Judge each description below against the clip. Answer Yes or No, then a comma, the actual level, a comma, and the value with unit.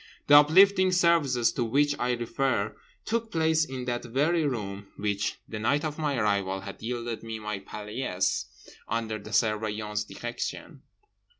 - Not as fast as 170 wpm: Yes, average, 145 wpm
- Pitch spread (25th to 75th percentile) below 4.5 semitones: No, wide, 5.6 semitones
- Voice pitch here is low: Yes, low, 120 Hz